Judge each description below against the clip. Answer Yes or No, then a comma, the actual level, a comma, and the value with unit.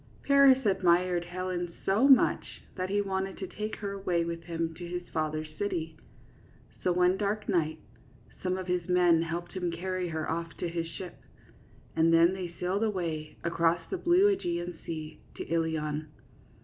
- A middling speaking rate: Yes, average, 165 wpm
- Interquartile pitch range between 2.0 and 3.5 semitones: Yes, narrow, 2.4 semitones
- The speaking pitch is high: No, medium, 175 Hz